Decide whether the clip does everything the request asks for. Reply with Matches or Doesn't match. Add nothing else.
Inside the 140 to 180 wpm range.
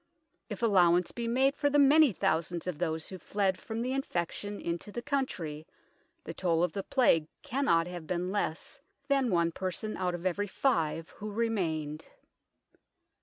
Matches